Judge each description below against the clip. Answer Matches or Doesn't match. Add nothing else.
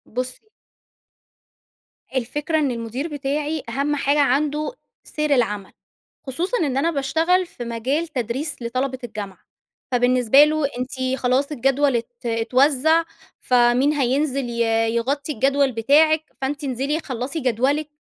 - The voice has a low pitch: Doesn't match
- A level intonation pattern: Doesn't match